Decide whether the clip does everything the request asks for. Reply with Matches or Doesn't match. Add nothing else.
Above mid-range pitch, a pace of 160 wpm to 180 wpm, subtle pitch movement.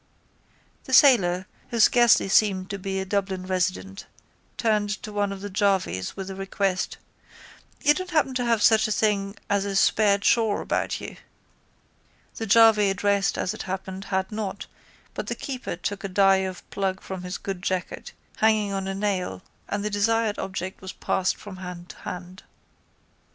Matches